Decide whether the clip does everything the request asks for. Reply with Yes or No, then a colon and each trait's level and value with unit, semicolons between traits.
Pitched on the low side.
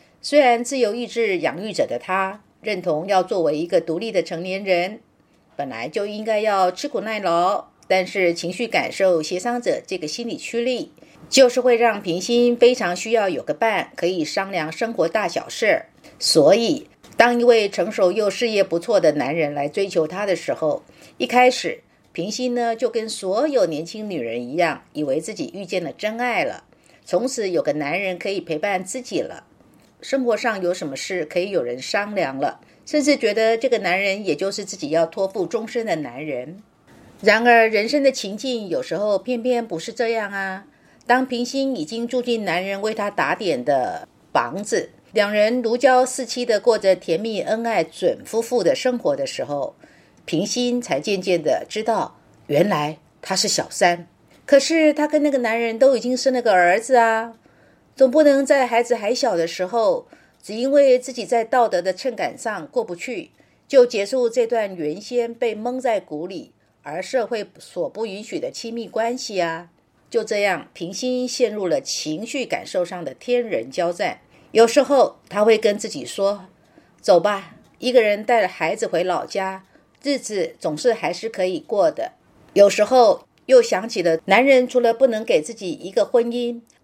No: high, 220 Hz